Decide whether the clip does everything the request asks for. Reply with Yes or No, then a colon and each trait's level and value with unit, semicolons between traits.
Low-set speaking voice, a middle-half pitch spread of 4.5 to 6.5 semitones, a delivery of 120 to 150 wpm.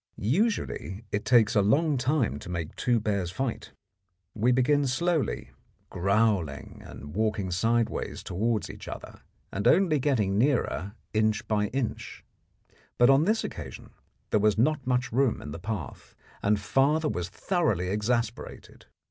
Yes: low, 110 Hz; average, 5.1 semitones; average, 140 wpm